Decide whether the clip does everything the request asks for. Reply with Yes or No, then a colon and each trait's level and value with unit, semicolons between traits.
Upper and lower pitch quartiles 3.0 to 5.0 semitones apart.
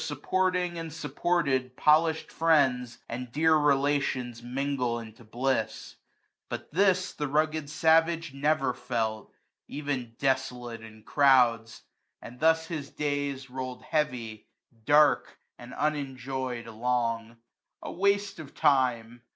Yes: average, 4.2 semitones